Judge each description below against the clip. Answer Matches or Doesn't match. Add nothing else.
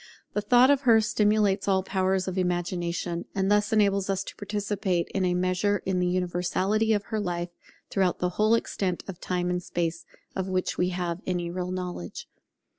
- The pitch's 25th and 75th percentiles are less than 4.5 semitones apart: Matches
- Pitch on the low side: Doesn't match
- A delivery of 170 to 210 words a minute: Matches